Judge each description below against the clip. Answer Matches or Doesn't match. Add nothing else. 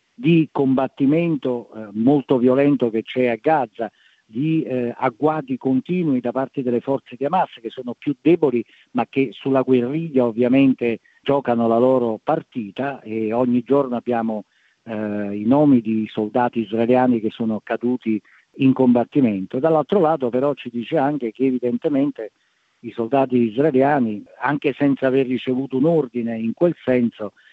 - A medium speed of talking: Matches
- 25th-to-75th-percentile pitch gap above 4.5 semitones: Doesn't match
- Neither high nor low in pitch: Doesn't match